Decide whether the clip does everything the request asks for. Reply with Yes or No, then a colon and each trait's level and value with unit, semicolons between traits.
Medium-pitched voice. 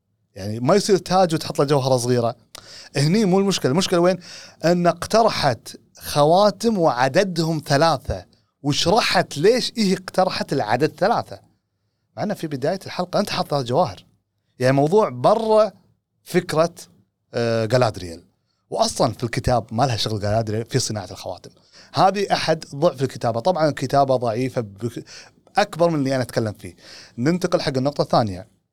Yes: medium, 145 Hz